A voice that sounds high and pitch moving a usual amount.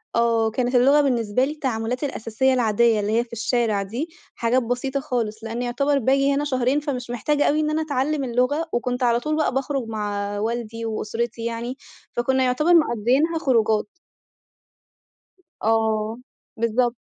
Yes: high, 245 Hz; average, 3.2 semitones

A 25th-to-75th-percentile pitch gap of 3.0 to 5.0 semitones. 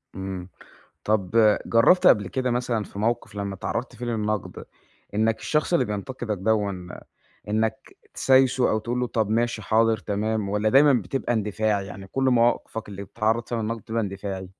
No: narrow, 2.6 semitones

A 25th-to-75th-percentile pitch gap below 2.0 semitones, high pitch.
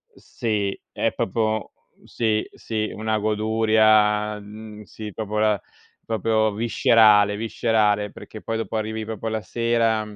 No: narrow, 0.9 semitones; low, 110 Hz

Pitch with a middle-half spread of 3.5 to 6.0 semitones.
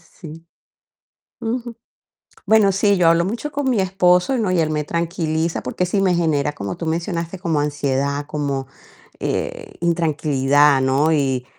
Yes: average, 4.6 semitones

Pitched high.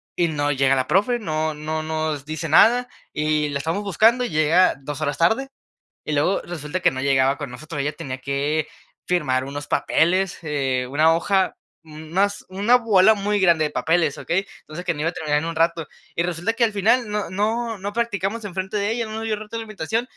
No: medium, 165 Hz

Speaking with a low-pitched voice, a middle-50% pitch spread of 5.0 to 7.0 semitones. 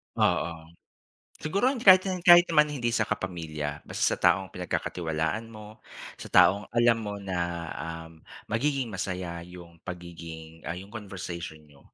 Yes: very low, 90 Hz; wide, 5.6 semitones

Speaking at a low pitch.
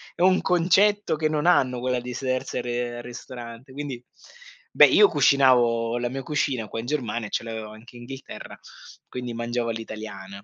Yes: low, 125 Hz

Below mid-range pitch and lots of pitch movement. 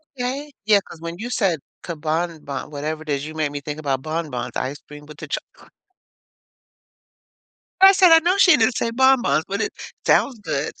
No: medium, 165 Hz; wide, 8.8 semitones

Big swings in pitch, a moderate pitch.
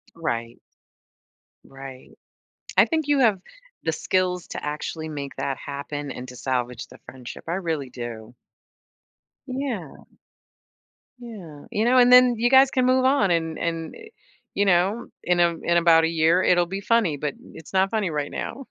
Yes: wide, 7.6 semitones; medium, 170 Hz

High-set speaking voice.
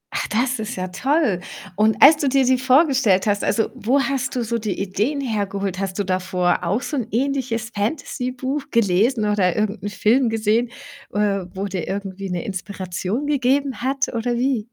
Yes: high, 220 Hz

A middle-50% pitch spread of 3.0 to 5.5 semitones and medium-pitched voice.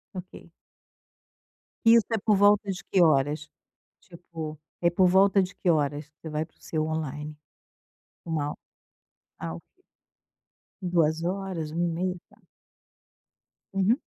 Yes: average, 3.7 semitones; medium, 170 Hz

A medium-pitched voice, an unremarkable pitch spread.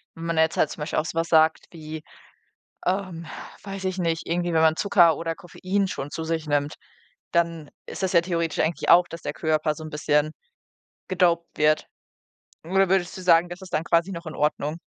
No: medium, 165 Hz; narrow, 2.0 semitones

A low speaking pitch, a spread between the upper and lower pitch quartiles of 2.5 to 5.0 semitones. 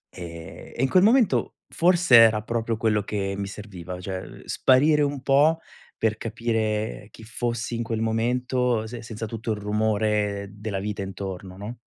Yes: low, 110 Hz; average, 2.9 semitones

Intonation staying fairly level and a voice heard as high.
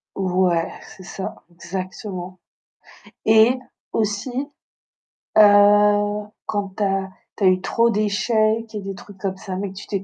Yes: narrow, 2.1 semitones; high, 205 Hz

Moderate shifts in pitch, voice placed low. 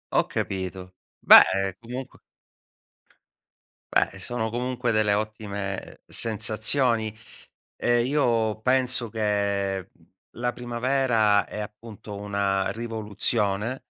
Yes: average, 3.0 semitones; low, 110 Hz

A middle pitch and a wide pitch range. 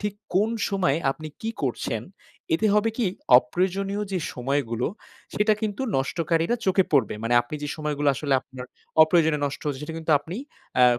Yes: medium, 155 Hz; wide, 6.0 semitones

